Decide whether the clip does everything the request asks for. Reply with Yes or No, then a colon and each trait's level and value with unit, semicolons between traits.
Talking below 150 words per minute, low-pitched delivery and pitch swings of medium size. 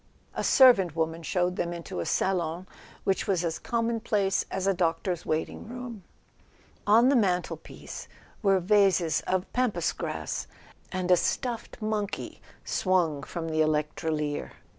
No: average, 140 wpm; medium, 185 Hz; average, 4.2 semitones